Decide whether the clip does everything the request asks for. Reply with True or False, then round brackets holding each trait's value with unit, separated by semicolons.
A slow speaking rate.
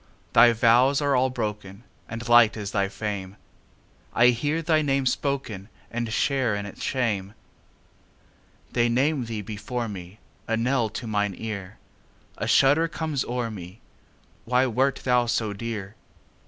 True (120 wpm)